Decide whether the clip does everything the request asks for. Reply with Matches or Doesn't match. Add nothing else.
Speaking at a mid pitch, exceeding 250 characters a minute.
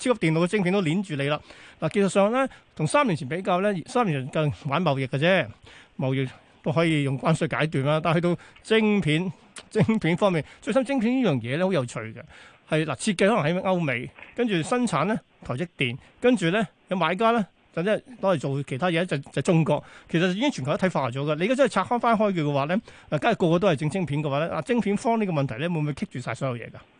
Matches